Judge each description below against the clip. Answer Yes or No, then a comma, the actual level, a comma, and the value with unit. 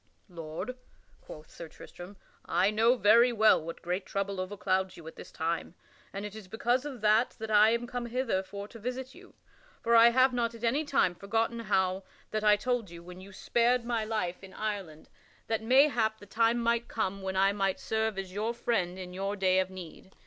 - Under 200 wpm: No, fast, 205 wpm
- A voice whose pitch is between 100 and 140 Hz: No, high, 210 Hz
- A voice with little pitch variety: No, average, 3.7 semitones